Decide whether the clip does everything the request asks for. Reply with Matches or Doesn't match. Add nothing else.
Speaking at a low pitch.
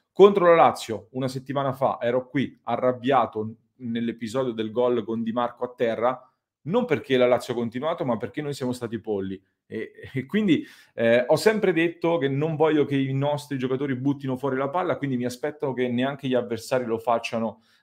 Matches